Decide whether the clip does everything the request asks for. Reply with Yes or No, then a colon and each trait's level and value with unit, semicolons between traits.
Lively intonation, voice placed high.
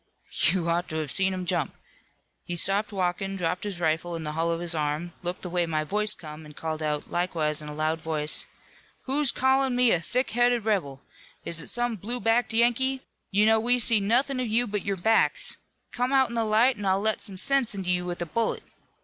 Yes: wide, 5.8 semitones; high, 195 Hz